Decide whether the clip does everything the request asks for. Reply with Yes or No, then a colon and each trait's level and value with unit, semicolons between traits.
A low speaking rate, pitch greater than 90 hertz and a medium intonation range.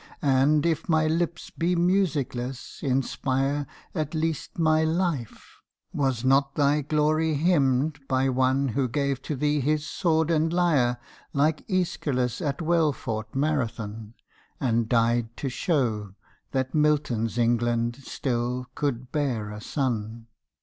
Yes: slow, 130 wpm; medium, 140 Hz; average, 4.3 semitones